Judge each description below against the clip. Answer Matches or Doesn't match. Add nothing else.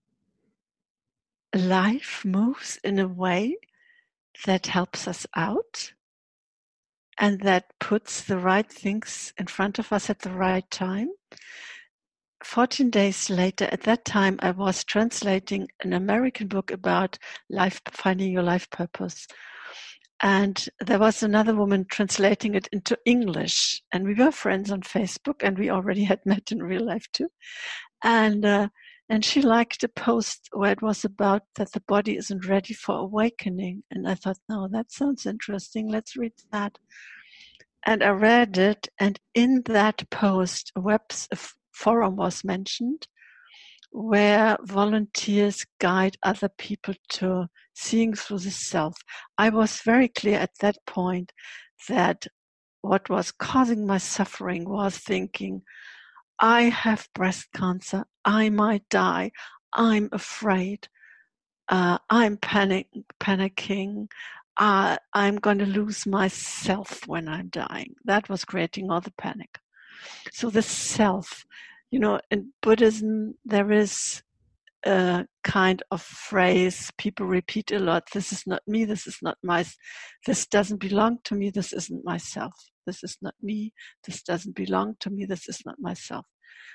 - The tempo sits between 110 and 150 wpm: Matches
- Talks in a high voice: Matches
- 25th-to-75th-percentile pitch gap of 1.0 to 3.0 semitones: Matches